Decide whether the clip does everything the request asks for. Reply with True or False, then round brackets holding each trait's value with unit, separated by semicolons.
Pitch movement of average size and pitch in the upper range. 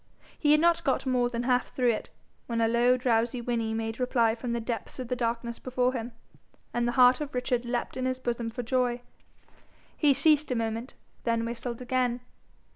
False (1.5 semitones; 245 Hz)